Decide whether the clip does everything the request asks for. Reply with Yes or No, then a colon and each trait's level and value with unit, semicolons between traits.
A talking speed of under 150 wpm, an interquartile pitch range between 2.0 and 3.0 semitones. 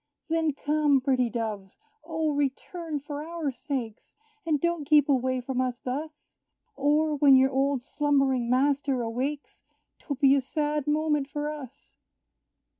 Yes: average, 140 wpm; narrow, 2.4 semitones